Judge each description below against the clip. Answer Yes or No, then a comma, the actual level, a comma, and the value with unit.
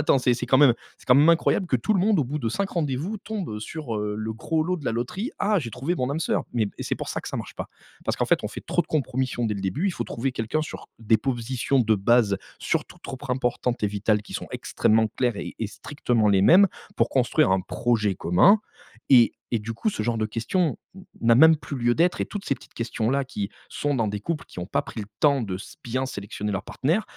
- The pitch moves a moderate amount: No, wide, 5.9 semitones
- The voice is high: No, low, 125 Hz